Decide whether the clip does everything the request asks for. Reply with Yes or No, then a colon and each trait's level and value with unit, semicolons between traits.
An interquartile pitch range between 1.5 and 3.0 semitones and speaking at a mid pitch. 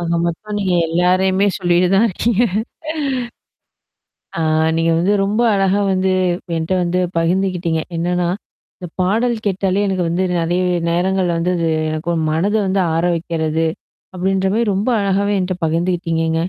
Yes: narrow, 2.5 semitones; medium, 180 Hz